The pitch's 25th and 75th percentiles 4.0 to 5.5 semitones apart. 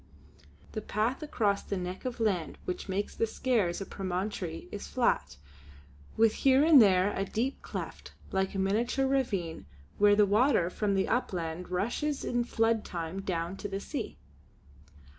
Yes: average, 4.4 semitones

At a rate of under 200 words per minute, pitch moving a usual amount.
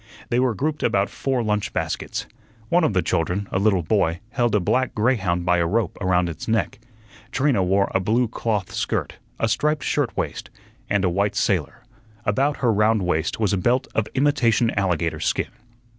Yes: average, 185 wpm; average, 4.6 semitones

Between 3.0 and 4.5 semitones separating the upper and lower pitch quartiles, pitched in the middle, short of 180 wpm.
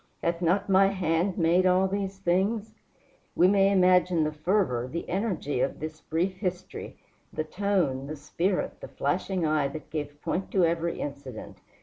Yes: average, 3.7 semitones; medium, 180 Hz; average, 160 wpm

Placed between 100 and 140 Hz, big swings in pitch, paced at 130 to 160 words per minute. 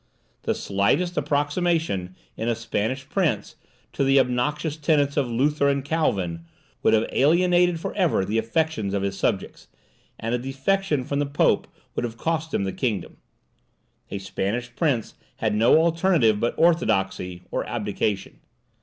Yes: low, 135 Hz; wide, 6.7 semitones; average, 150 wpm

